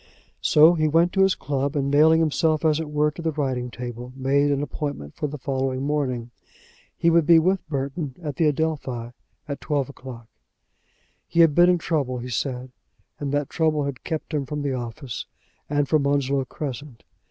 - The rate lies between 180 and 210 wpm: Yes, average, 185 wpm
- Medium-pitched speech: Yes, medium, 145 Hz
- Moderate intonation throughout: Yes, average, 3.0 semitones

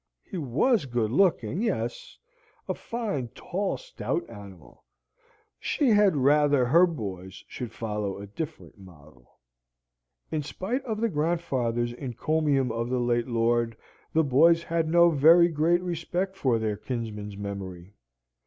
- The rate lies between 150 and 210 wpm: No, slow, 135 wpm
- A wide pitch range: Yes, wide, 7.1 semitones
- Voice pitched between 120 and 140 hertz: Yes, low, 135 Hz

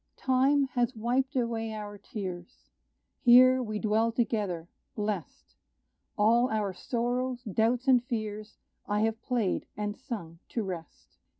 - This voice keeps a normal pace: No, slow, 125 wpm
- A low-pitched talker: No, high, 225 Hz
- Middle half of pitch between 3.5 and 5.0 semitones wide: No, average, 3.0 semitones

